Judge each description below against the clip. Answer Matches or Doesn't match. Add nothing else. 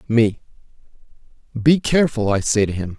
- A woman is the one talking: Doesn't match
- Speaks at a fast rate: Doesn't match